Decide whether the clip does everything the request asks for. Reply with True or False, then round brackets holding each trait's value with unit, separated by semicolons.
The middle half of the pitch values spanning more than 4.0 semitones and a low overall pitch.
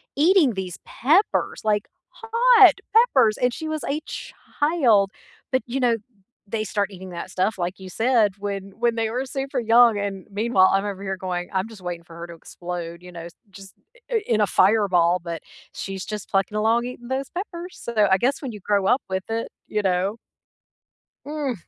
False (5.1 semitones; 210 Hz)